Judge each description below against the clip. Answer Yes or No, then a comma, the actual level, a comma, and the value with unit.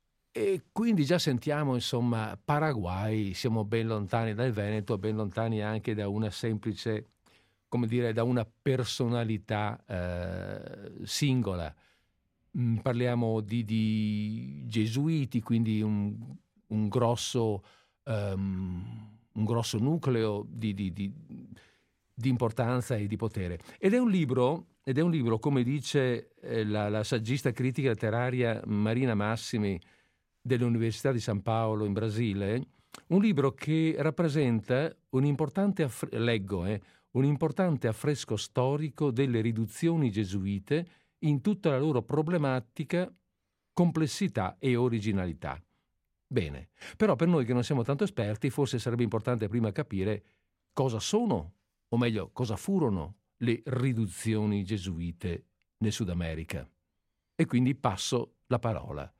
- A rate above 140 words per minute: No, average, 125 wpm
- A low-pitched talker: Yes, low, 115 Hz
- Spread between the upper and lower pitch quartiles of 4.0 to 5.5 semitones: Yes, average, 4.3 semitones